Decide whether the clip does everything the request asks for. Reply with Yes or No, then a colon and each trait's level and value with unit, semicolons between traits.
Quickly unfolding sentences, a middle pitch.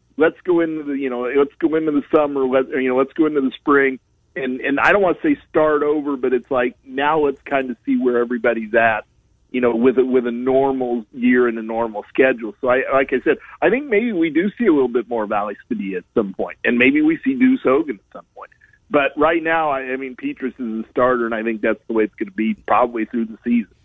No: fast, 260 wpm; low, 130 Hz